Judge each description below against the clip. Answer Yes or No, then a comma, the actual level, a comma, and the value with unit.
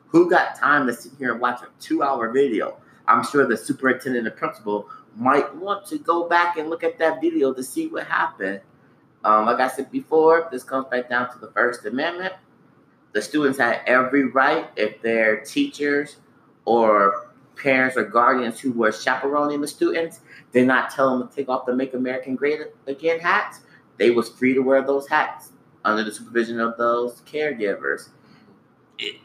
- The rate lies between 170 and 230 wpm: Yes, average, 180 wpm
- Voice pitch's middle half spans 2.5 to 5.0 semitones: Yes, average, 4.1 semitones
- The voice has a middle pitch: No, low, 130 Hz